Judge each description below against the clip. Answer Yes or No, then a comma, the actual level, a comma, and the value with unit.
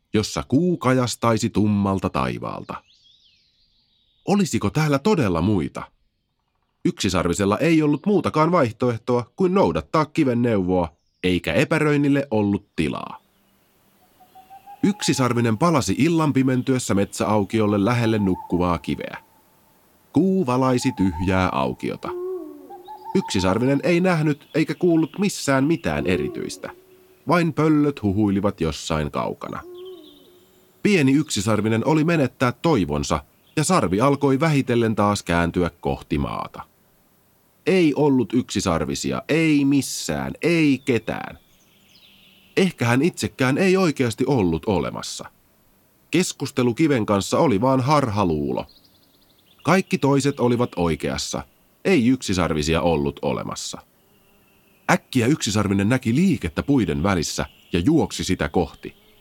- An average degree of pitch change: No, wide, 8.4 semitones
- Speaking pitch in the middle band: No, low, 125 Hz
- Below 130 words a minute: Yes, average, 100 wpm